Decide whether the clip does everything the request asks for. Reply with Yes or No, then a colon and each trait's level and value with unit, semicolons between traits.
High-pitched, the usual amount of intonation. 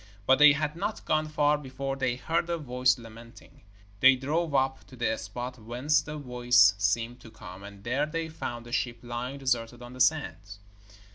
No: low, 130 Hz; average, 3.7 semitones